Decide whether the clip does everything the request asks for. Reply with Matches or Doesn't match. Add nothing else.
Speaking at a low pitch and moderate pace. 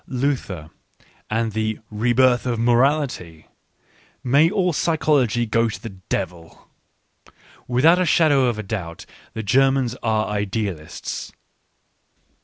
Doesn't match